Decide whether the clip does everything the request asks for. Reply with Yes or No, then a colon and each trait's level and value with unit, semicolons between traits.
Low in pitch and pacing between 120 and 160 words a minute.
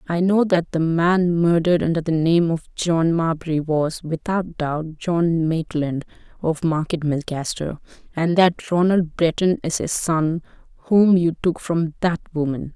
No: medium, 165 Hz; average, 155 wpm